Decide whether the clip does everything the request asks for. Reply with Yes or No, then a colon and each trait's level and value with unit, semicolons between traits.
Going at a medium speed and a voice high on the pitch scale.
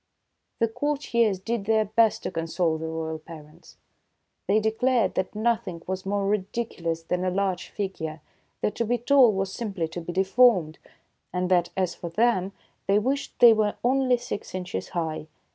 Yes: average, 165 wpm; high, 195 Hz